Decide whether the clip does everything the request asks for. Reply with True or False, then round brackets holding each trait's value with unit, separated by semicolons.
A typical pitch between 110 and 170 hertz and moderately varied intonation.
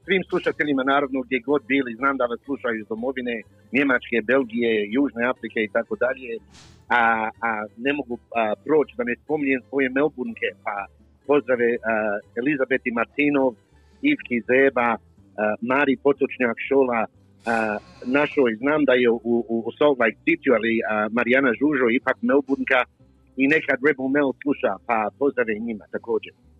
True (125 Hz; 3.6 semitones)